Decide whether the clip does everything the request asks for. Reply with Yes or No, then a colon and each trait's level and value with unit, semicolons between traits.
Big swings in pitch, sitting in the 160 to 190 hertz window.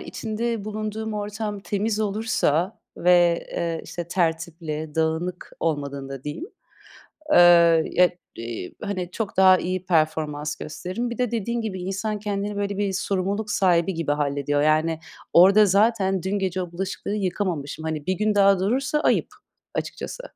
No: average, 4.3 semitones; medium, 185 Hz